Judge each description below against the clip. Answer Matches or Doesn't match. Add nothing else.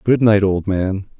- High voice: Doesn't match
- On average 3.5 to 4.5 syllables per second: Matches